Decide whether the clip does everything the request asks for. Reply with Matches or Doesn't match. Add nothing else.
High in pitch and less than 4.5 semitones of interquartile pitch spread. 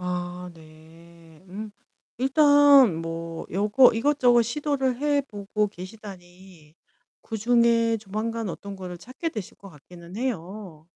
Doesn't match